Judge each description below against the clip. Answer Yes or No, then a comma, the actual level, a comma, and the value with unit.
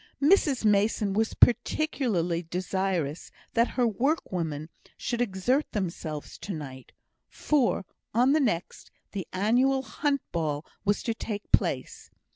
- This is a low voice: No, high, 205 Hz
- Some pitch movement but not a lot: No, wide, 6.4 semitones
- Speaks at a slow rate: Yes, slow, 120 wpm